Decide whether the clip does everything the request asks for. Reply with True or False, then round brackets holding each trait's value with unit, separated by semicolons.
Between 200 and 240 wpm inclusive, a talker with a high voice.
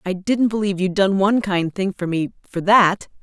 True (205 wpm; 195 Hz)